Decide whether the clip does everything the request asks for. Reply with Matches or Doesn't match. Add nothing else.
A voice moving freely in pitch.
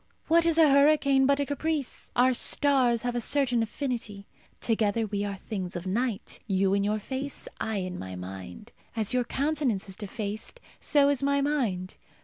Matches